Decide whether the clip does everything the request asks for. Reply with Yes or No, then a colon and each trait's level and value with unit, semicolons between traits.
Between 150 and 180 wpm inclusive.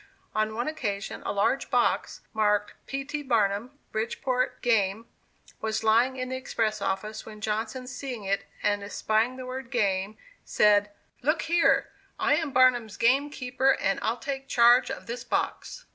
Yes: average, 160 wpm